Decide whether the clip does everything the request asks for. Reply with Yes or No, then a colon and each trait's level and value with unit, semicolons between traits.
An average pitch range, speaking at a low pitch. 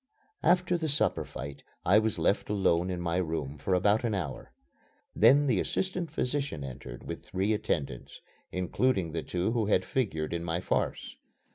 No: wide, 6.6 semitones; very low, 95 Hz